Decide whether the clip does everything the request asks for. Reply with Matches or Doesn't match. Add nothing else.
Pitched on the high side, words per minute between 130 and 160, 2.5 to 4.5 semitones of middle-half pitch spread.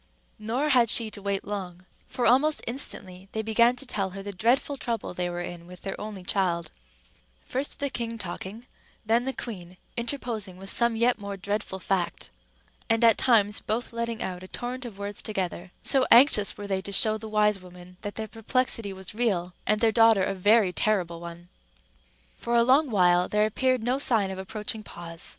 Doesn't match